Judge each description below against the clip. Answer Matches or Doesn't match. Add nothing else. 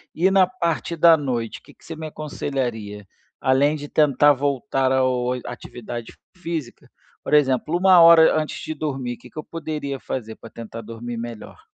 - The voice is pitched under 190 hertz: Matches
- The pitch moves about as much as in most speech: Matches